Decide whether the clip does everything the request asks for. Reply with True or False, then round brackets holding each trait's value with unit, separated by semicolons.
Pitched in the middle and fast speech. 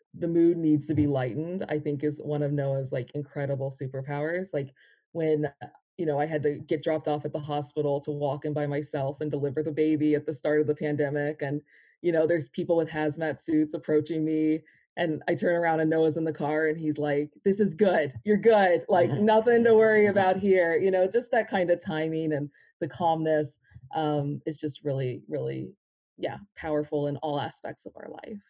True (155 Hz; 210 wpm)